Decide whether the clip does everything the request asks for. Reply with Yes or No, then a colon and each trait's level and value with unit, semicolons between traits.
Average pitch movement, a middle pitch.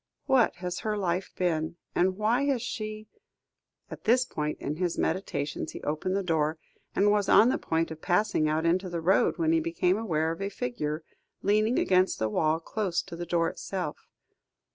Yes: average, 4.3 semitones; medium, 180 Hz